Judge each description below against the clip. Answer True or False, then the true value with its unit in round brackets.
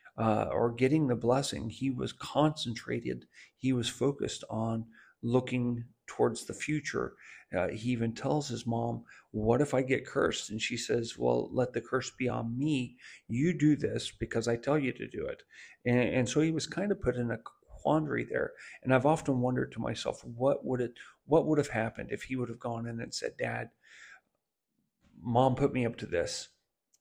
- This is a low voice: True (125 Hz)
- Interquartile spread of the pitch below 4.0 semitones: True (3.2 semitones)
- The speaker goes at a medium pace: True (195 wpm)